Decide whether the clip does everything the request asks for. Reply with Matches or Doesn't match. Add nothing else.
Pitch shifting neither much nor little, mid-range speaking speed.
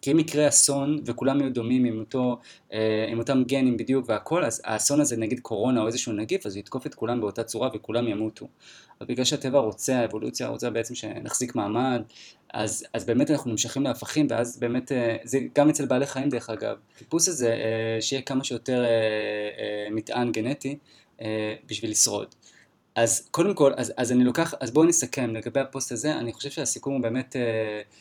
Doesn't match